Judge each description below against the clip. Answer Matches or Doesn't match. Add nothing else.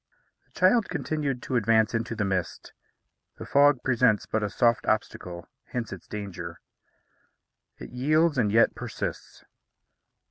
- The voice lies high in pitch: Doesn't match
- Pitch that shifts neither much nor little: Matches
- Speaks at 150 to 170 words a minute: Doesn't match